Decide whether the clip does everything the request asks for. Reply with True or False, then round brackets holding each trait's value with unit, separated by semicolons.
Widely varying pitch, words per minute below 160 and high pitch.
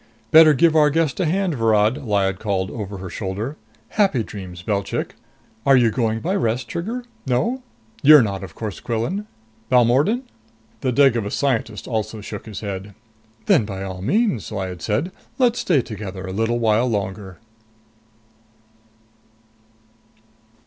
False (6.5 semitones; 140 wpm; 115 Hz)